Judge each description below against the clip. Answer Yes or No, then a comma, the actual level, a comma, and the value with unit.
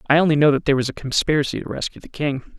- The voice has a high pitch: No, medium, 145 Hz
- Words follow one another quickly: Yes, fast, 280 wpm